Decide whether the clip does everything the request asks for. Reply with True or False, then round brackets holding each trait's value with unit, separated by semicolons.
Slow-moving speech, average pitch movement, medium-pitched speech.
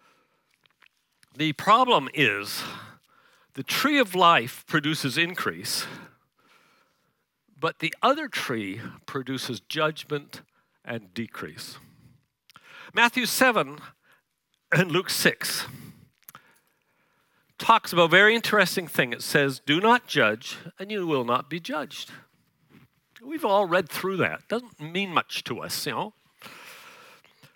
False (115 wpm; 8.8 semitones; 170 Hz)